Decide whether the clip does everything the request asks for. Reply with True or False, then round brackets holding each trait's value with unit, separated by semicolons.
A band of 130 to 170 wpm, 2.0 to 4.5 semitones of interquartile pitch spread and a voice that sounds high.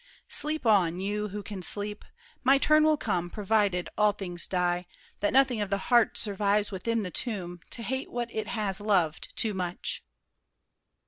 True (160 wpm; 3.7 semitones; 205 Hz)